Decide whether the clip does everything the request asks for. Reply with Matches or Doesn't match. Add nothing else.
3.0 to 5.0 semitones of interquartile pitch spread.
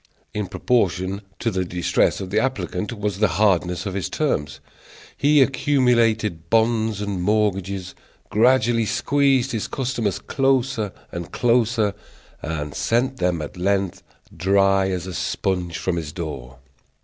Matches